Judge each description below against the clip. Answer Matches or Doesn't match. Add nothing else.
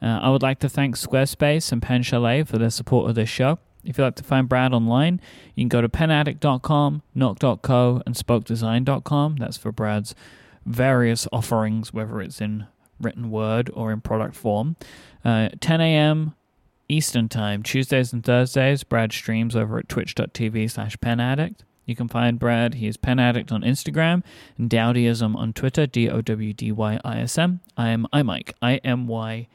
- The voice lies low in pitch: Matches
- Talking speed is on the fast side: Doesn't match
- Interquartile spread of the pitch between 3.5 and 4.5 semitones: Doesn't match